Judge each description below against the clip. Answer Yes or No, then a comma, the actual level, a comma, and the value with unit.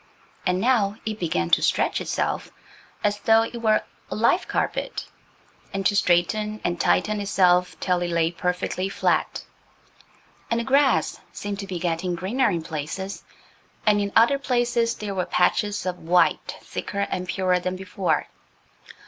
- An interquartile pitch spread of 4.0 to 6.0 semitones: No, average, 3.2 semitones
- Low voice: No, high, 195 Hz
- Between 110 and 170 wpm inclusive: Yes, average, 155 wpm